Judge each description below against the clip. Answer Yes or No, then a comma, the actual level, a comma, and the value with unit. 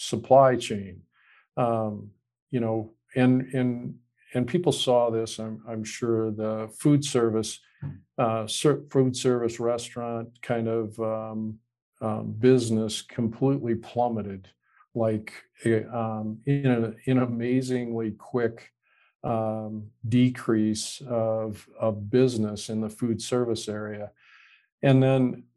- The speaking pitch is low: Yes, low, 115 Hz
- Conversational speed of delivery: No, slow, 110 wpm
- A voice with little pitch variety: Yes, narrow, 2.2 semitones